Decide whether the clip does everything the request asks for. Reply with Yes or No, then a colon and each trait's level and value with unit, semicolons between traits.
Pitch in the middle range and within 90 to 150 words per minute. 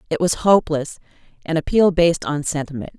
Yes: medium, 160 Hz; average, 140 wpm